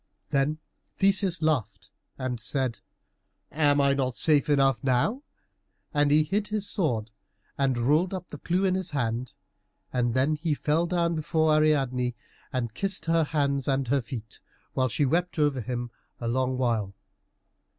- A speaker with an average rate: Yes, average, 155 wpm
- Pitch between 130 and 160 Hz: Yes, medium, 140 Hz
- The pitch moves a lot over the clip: No, average, 4.1 semitones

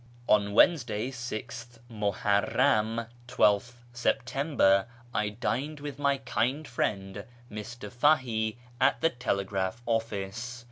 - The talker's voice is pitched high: No, low, 115 Hz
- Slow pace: Yes, slow, 100 wpm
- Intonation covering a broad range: No, average, 3.3 semitones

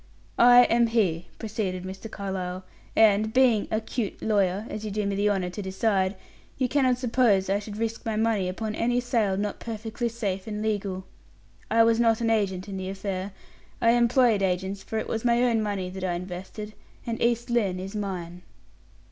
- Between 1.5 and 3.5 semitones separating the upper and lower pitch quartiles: Yes, average, 3.1 semitones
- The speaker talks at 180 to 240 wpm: Yes, average, 190 wpm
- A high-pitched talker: Yes, high, 210 Hz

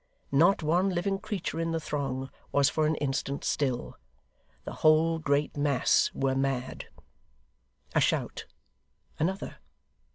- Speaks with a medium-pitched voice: Yes, medium, 150 Hz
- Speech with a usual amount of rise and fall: Yes, average, 3.3 semitones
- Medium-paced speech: No, slow, 125 wpm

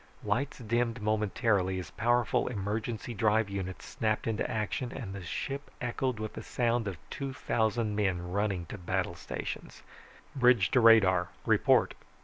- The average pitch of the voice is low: Yes, low, 110 Hz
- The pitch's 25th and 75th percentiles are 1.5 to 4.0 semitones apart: Yes, average, 3.4 semitones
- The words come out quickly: No, average, 145 wpm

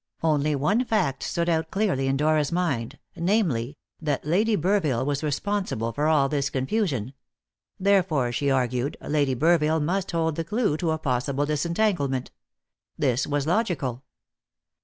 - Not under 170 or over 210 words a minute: No, average, 140 wpm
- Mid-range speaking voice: Yes, medium, 150 Hz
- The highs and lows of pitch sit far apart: No, average, 4.4 semitones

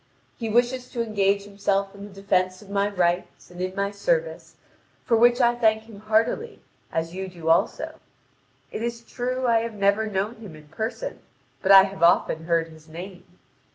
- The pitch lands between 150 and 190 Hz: No, high, 200 Hz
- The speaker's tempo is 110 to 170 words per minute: No, average, 185 wpm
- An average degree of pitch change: Yes, average, 3.7 semitones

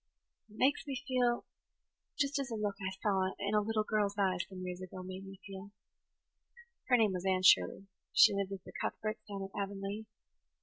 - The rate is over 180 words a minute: Yes, average, 200 wpm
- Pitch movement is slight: Yes, narrow, 2.2 semitones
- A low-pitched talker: No, high, 200 Hz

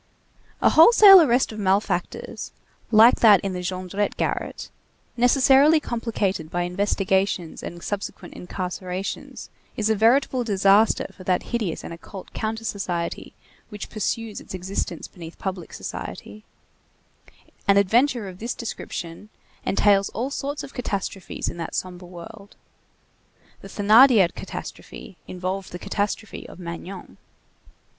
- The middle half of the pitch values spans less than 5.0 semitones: Yes, average, 3.7 semitones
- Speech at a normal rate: No, slow, 125 wpm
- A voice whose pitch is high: Yes, high, 200 Hz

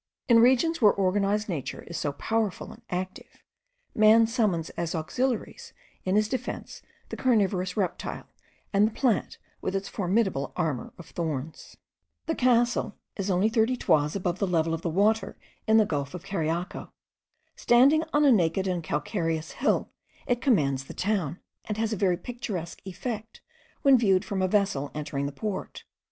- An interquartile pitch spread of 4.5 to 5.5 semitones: Yes, average, 4.9 semitones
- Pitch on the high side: Yes, high, 195 Hz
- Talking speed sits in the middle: Yes, average, 165 wpm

